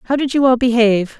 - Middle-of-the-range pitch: No, high, 245 Hz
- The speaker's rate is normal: No, fast, 250 wpm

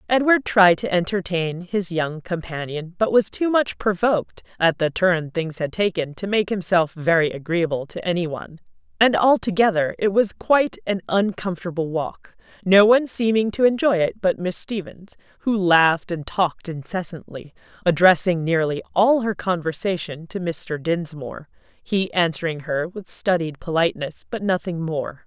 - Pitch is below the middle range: No, medium, 180 Hz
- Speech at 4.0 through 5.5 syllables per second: Yes, 4.8 syllables/s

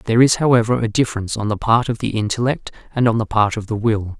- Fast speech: Yes, fast, 260 wpm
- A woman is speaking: No, male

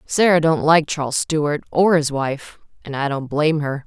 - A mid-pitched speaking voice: Yes, medium, 150 Hz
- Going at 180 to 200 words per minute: Yes, average, 185 wpm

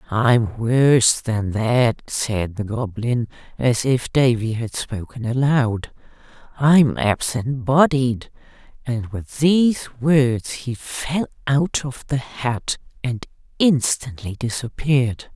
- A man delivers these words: No, female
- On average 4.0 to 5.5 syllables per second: No, 3.3 syllables/s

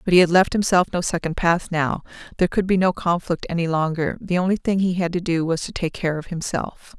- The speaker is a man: No, female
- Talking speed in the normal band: No, fast, 250 wpm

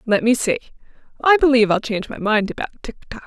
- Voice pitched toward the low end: No, high, 235 Hz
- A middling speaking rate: No, fast, 220 wpm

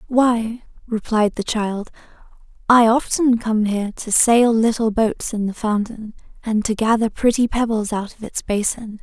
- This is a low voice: No, high, 220 Hz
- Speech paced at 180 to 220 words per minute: No, average, 160 wpm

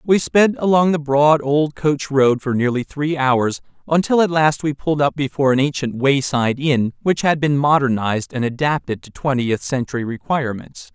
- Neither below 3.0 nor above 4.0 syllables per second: No, 5.1 syllables/s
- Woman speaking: No, male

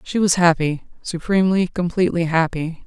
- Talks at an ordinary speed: No, slow, 105 wpm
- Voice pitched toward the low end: No, medium, 175 Hz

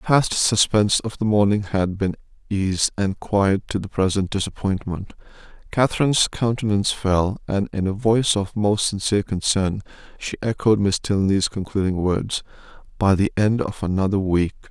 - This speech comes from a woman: No, male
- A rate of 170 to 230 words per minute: No, average, 155 wpm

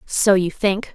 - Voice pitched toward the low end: No, high, 195 Hz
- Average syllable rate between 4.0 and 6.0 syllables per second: No, 3.5 syllables/s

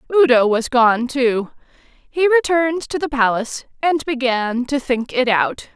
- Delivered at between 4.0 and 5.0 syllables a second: Yes, 4.3 syllables/s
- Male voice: No, female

